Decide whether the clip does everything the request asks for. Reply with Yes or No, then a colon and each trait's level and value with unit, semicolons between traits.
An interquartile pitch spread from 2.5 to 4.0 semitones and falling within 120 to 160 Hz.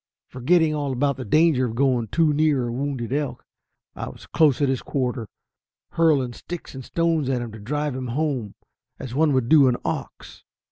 Yes: average, 3.5 semitones; low, 135 Hz